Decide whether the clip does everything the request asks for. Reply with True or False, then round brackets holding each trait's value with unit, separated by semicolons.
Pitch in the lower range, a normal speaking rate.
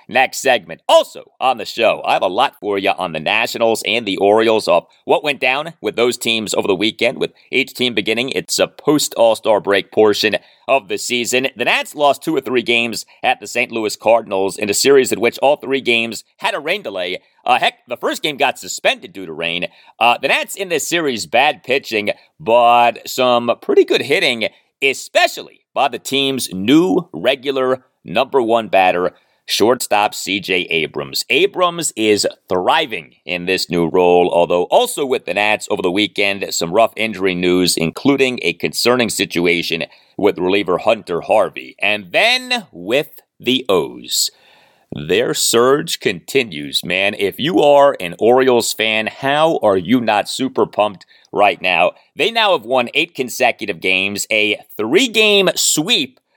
True (120 Hz; 170 wpm)